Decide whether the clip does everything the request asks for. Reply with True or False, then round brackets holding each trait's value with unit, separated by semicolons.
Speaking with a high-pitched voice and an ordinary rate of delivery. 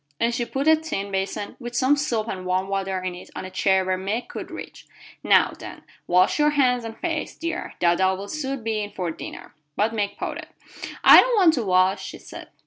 False (210 Hz; 220 wpm)